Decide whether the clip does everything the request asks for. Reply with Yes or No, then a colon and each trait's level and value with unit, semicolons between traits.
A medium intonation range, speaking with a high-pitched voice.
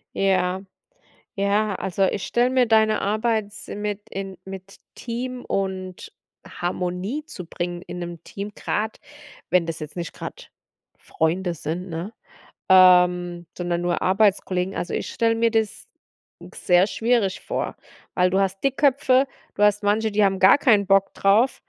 Yes: average, 3.3 semitones; high, 195 Hz